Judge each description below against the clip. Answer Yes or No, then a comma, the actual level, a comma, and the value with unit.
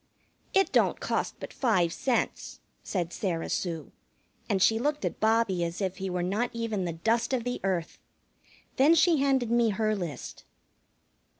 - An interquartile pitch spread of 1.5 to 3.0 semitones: No, average, 5.2 semitones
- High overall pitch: Yes, high, 215 Hz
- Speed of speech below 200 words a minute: Yes, average, 165 wpm